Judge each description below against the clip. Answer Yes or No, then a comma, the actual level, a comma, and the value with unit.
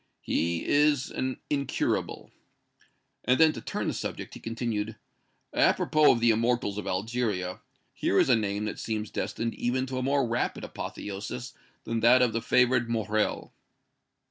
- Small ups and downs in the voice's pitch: No, average, 3.1 semitones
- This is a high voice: No, low, 115 Hz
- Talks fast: No, average, 160 wpm